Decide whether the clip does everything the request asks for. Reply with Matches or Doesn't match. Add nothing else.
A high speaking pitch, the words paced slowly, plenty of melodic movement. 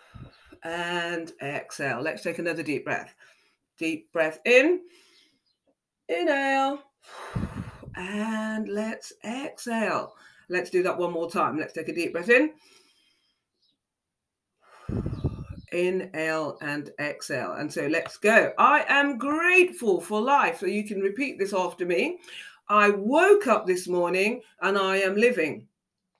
Matches